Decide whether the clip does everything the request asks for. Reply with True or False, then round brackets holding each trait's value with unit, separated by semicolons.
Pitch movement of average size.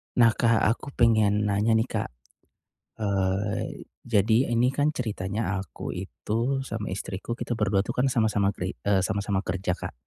True (3.0 semitones)